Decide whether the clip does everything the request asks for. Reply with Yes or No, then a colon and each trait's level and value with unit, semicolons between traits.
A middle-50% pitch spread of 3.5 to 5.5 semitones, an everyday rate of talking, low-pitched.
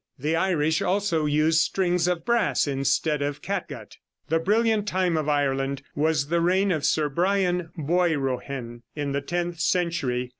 No: average, 4.0 semitones; average, 150 wpm; medium, 160 Hz